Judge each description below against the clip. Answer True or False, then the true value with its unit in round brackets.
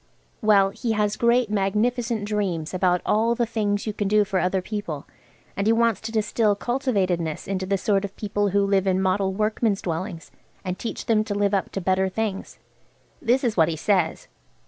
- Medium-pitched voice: False (205 Hz)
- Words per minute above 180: True (190 wpm)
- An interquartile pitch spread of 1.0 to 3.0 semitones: True (2.5 semitones)